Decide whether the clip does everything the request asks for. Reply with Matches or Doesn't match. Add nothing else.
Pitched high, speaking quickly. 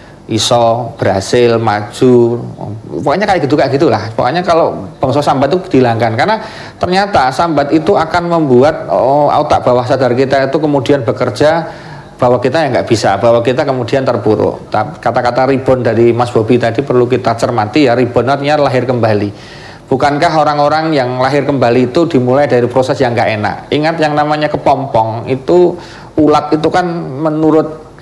Doesn't match